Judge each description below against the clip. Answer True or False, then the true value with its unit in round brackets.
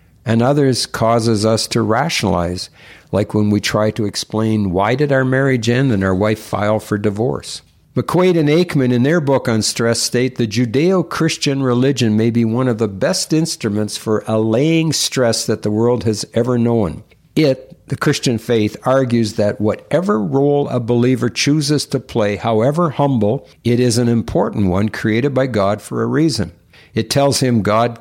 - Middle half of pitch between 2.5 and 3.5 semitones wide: False (4.2 semitones)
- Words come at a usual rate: True (175 wpm)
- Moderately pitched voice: False (120 Hz)